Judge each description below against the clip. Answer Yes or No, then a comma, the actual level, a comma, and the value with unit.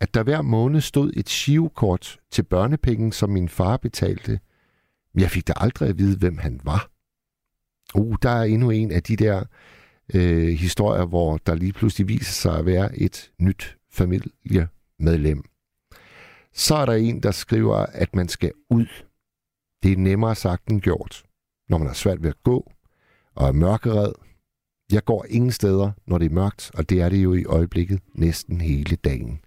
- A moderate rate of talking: Yes, average, 180 wpm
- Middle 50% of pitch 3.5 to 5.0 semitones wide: Yes, average, 4.3 semitones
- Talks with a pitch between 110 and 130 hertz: No, very low, 95 Hz